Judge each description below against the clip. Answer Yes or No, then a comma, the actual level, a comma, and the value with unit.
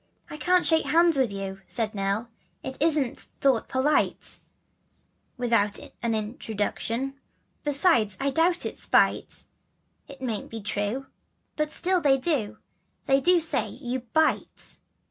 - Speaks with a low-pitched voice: No, very high, 260 Hz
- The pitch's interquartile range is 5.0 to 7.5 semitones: Yes, wide, 5.5 semitones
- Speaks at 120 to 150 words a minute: Yes, average, 140 wpm